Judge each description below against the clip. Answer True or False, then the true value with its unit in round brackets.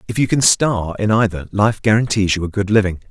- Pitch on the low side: True (105 Hz)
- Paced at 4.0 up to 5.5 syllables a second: False (5.7 syllables/s)